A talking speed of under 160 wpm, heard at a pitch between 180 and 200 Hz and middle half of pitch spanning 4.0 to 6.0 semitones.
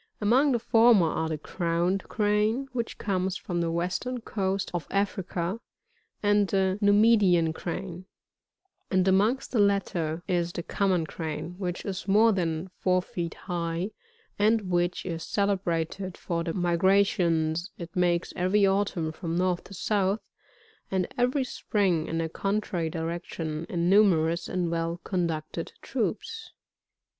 No: slow, 135 wpm; medium, 185 Hz; average, 3.2 semitones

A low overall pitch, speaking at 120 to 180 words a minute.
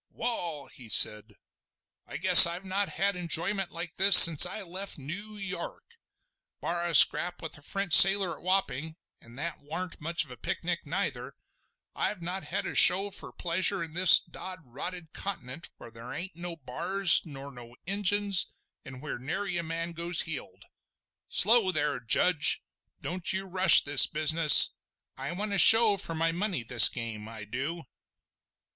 No: medium, 170 Hz; average, 160 wpm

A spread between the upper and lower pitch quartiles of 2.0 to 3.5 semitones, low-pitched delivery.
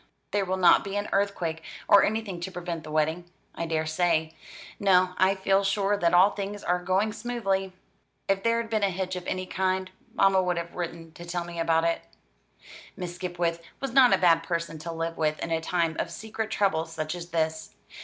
No: average, 2.7 semitones; medium, 180 Hz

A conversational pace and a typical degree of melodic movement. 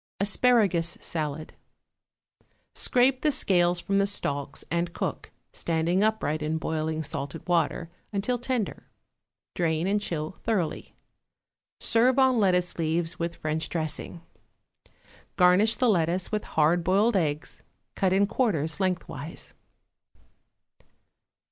No: slow, 110 wpm; average, 4.3 semitones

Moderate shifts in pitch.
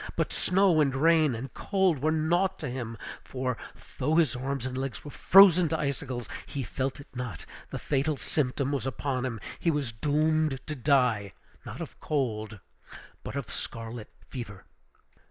Yes: average, 3.9 semitones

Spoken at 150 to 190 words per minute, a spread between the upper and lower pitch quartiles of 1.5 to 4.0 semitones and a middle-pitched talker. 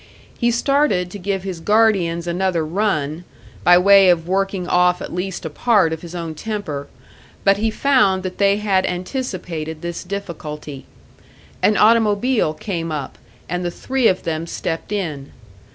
Yes: average, 155 wpm; average, 3.6 semitones; medium, 180 Hz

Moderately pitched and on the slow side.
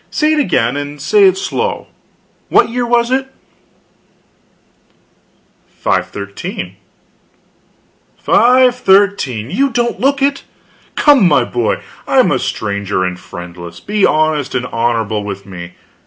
Yes: medium, 155 Hz; slow, 120 wpm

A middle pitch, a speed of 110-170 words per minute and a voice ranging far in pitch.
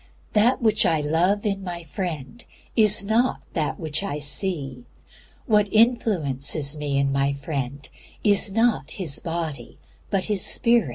Yes: medium, 170 Hz; average, 140 wpm; wide, 6.6 semitones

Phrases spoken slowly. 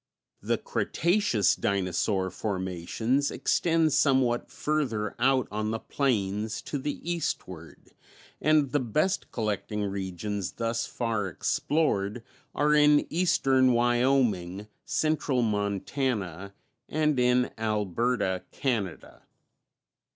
Yes: slow, 95 wpm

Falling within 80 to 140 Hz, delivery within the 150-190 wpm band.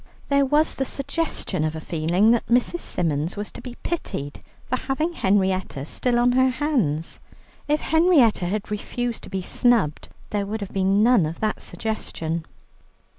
No: high, 215 Hz; average, 165 wpm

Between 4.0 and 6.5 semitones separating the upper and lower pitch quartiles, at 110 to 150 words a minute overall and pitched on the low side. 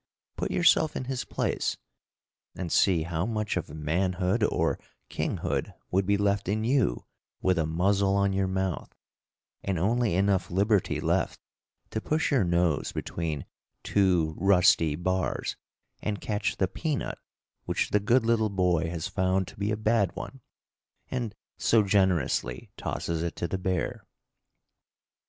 No: average, 3.3 semitones; average, 145 wpm; very low, 95 Hz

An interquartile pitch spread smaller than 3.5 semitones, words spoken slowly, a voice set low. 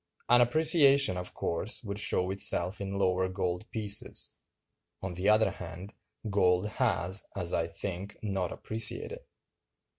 Yes: average, 3.0 semitones; slow, 130 wpm; low, 100 Hz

